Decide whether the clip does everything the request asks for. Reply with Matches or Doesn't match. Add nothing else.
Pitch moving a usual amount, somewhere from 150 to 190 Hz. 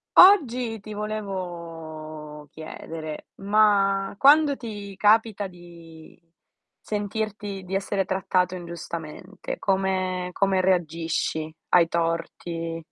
Matches